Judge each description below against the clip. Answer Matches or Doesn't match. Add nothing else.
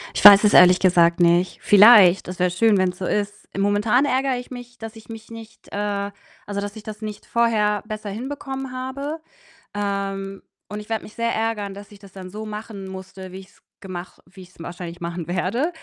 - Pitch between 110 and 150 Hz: Doesn't match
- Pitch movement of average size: Matches